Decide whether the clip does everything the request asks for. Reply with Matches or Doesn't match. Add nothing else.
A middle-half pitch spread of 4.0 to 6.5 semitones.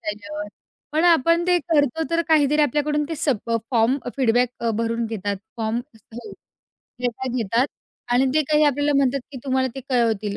Matches